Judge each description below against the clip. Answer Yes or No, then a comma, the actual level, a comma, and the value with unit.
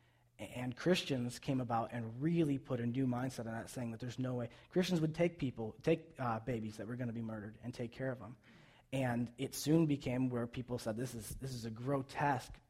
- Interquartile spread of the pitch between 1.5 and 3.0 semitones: Yes, narrow, 2.4 semitones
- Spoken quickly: Yes, fast, 225 wpm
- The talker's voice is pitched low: Yes, low, 125 Hz